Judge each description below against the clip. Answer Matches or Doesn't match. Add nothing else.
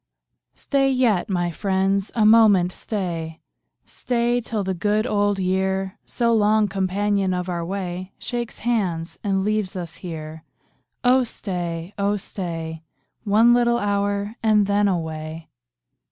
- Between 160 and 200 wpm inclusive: Doesn't match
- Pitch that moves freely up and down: Doesn't match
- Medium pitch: Doesn't match